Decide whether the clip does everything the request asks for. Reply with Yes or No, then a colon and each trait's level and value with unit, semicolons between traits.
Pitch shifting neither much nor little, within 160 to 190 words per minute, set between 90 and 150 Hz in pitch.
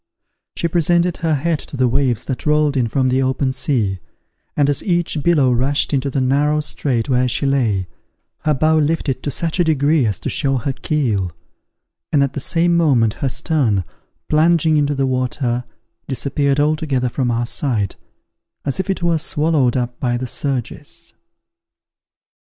Yes: average, 3.4 semitones; average, 170 wpm; medium, 140 Hz